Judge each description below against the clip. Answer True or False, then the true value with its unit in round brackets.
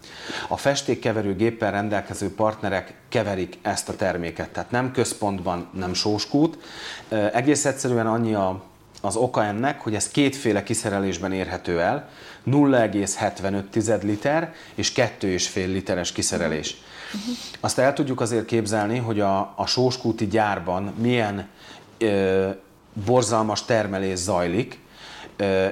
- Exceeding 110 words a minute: False (105 wpm)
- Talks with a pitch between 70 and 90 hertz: False (105 Hz)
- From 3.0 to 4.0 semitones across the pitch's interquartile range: True (3.4 semitones)